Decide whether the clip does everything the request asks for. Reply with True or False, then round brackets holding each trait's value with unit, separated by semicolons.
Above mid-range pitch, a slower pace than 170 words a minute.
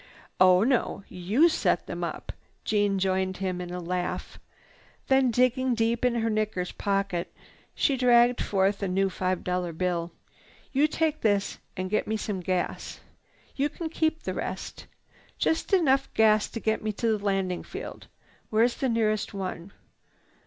True (210 Hz; 160 wpm)